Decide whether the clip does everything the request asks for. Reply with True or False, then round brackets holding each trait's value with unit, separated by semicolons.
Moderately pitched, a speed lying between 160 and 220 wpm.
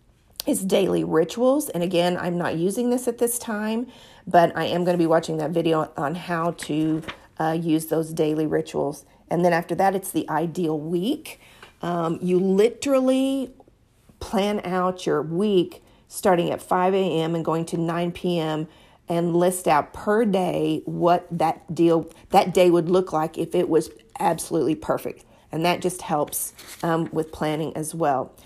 True (170 Hz; 170 wpm)